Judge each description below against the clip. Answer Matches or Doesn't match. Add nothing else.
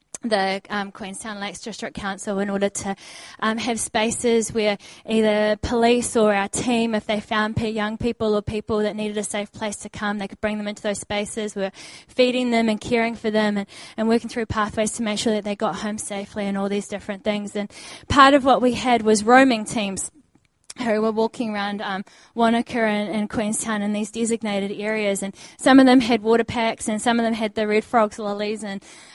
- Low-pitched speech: Doesn't match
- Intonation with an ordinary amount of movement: Doesn't match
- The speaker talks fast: Matches